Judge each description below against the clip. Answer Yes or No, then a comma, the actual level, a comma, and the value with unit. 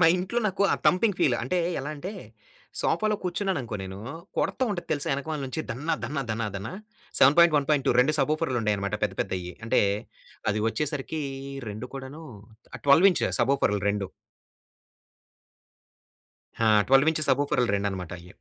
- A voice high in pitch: No, low, 135 Hz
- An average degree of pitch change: No, wide, 6.7 semitones